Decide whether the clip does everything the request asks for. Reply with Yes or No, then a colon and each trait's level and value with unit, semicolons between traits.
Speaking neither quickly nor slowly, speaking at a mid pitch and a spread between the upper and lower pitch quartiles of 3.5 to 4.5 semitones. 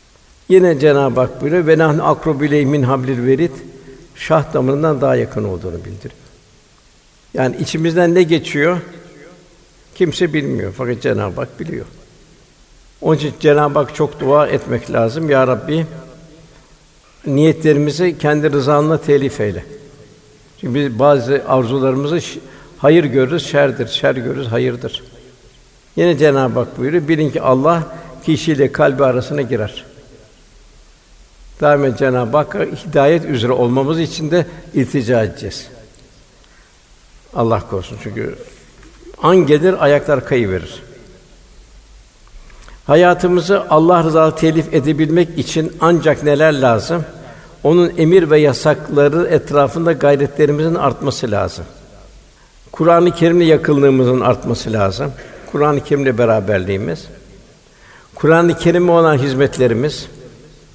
Yes: average, 105 wpm; medium, 145 Hz; average, 3.8 semitones